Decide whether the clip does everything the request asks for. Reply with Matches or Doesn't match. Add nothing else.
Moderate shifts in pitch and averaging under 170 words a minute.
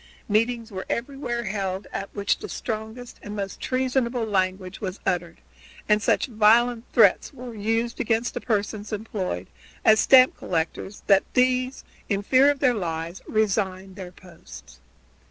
Matches